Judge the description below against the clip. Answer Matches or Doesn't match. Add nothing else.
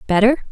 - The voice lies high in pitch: Matches